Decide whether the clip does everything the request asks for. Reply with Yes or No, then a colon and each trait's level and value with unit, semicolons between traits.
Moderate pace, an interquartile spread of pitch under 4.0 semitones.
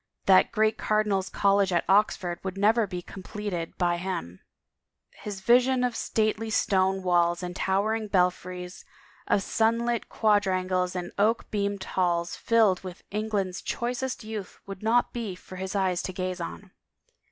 Yes: average, 150 wpm; average, 2.9 semitones